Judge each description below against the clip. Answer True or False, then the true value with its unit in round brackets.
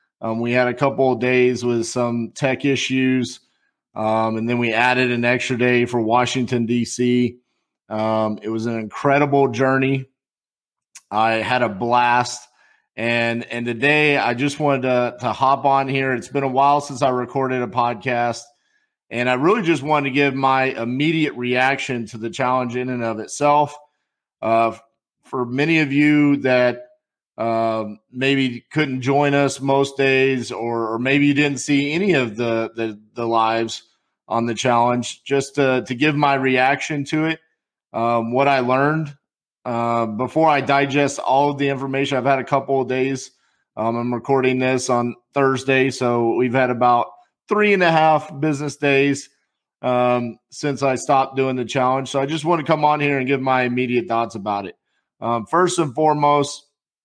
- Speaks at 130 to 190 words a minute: True (175 wpm)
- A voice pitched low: True (130 Hz)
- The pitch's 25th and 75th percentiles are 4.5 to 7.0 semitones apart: False (2.8 semitones)